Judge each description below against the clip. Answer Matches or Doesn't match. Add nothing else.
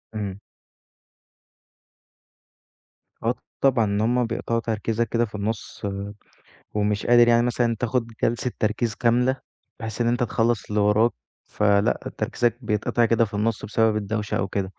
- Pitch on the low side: Matches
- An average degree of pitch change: Doesn't match